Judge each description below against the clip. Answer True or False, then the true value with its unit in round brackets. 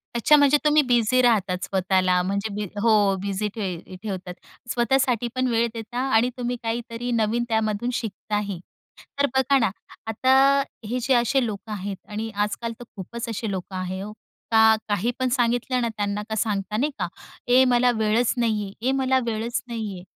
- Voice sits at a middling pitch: False (225 Hz)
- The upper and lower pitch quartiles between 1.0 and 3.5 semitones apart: True (3.1 semitones)